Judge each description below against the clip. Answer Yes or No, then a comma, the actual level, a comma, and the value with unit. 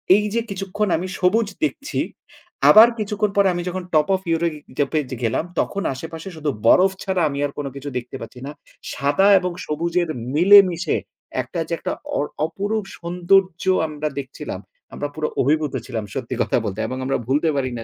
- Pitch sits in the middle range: Yes, medium, 170 Hz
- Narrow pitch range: No, average, 5.1 semitones